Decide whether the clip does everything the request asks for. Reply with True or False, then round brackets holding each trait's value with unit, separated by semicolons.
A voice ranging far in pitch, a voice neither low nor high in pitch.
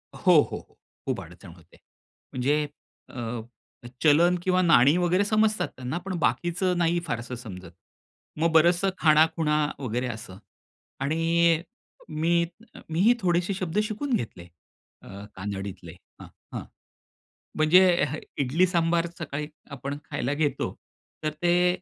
True (5.8 semitones; 160 Hz)